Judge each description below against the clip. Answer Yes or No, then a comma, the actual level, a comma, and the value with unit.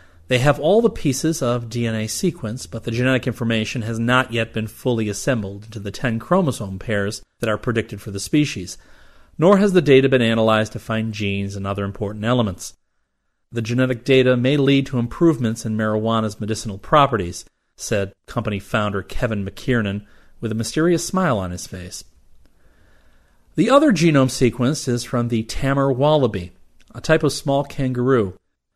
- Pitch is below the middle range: Yes, low, 115 Hz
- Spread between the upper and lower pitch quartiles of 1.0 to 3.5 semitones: No, average, 4.6 semitones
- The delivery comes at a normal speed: Yes, average, 165 wpm